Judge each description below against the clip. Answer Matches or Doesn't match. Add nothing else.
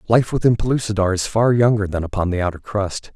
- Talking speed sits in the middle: Doesn't match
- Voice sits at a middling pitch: Doesn't match